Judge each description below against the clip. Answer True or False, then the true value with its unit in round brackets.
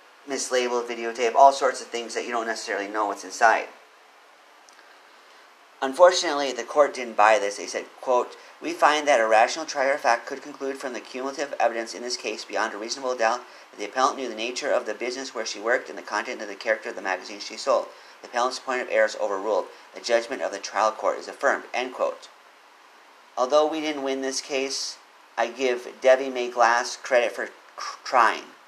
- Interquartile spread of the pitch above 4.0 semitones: False (2.8 semitones)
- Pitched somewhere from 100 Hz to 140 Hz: True (130 Hz)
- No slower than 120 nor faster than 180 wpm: False (205 wpm)